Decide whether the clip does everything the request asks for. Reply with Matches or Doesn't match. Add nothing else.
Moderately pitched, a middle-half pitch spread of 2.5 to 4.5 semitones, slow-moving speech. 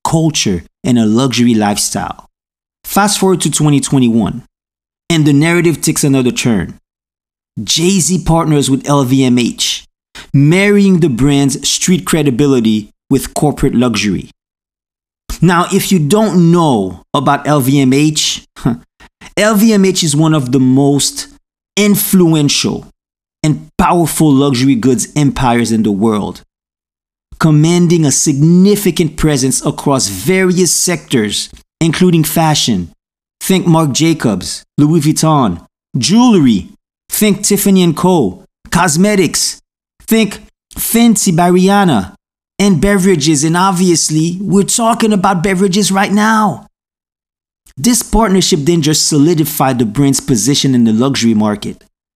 Doesn't match